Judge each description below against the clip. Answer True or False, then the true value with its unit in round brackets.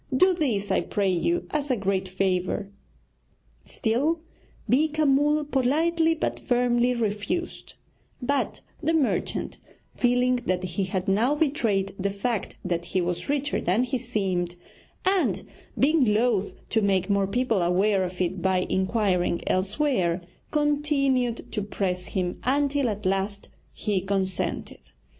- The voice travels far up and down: True (6.6 semitones)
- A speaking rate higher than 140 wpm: False (135 wpm)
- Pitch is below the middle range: False (215 Hz)